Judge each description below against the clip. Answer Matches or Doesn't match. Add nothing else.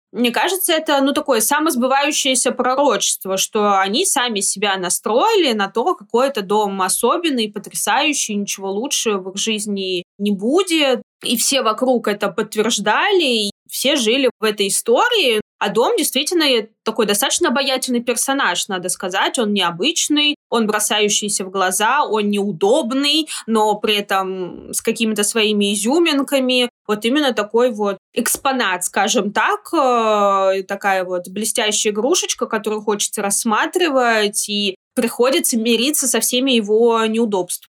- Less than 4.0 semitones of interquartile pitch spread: Doesn't match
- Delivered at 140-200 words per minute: Doesn't match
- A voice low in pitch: Doesn't match